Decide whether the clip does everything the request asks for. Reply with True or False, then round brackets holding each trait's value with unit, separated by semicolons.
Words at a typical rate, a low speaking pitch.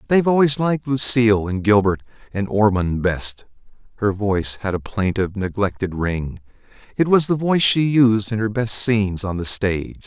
True (175 wpm; 110 Hz)